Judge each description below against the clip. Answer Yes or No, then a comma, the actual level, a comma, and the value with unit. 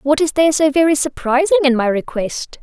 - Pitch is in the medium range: No, very high, 285 Hz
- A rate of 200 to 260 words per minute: Yes, fast, 205 wpm